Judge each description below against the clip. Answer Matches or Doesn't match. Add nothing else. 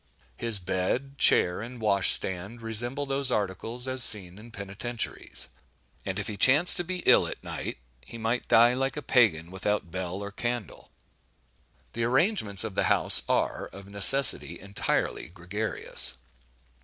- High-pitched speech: Doesn't match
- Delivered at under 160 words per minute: Matches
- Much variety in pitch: Doesn't match